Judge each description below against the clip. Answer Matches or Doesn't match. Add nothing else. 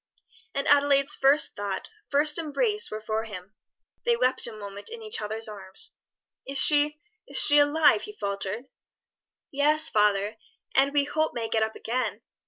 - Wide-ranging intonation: Matches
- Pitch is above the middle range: Matches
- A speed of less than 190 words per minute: Matches